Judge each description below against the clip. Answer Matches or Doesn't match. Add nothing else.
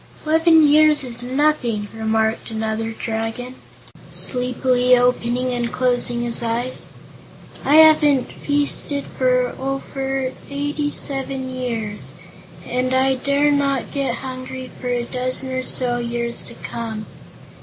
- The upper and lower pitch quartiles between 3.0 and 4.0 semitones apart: Doesn't match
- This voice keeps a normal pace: Doesn't match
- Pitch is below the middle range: Doesn't match